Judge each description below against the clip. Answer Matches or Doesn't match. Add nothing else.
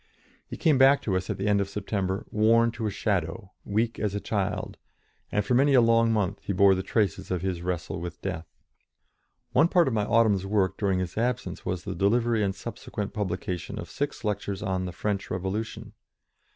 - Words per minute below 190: Doesn't match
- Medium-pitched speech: Doesn't match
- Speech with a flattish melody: Doesn't match